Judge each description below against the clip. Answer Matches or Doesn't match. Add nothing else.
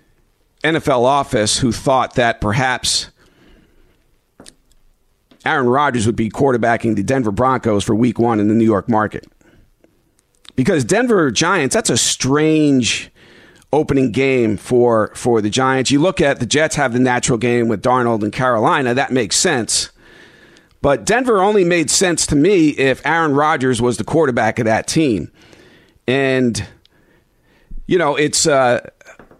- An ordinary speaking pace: Matches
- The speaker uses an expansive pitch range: Doesn't match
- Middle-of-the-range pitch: Doesn't match